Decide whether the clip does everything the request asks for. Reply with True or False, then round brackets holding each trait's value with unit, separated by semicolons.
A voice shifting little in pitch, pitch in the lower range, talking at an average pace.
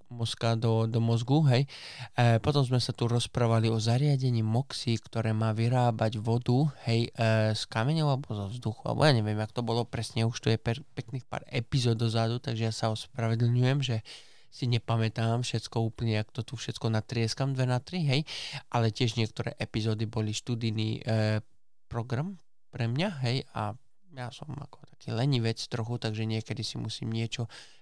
False (2.3 semitones; 115 Hz; 175 wpm)